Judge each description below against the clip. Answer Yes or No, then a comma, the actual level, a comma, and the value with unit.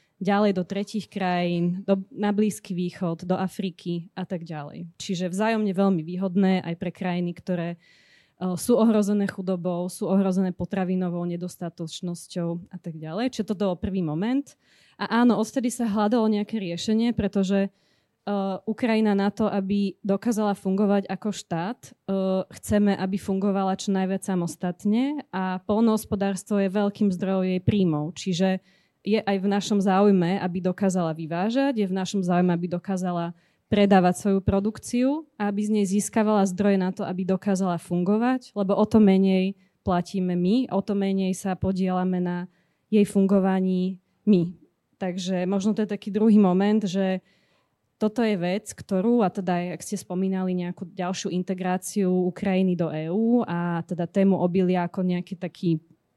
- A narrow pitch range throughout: Yes, narrow, 2.3 semitones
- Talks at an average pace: Yes, average, 155 wpm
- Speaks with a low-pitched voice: No, high, 190 Hz